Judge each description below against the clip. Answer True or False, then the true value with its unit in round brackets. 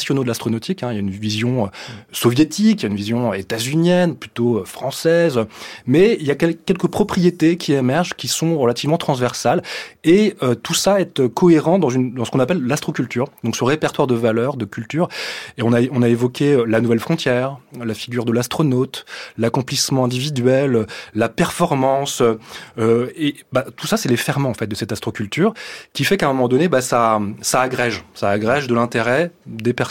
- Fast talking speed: False (190 wpm)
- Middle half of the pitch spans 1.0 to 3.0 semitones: False (4.8 semitones)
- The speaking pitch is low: True (125 Hz)